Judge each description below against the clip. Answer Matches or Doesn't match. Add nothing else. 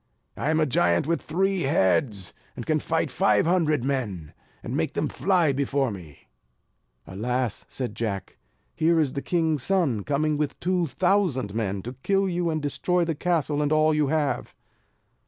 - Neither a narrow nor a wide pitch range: Doesn't match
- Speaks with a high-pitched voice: Doesn't match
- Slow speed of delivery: Doesn't match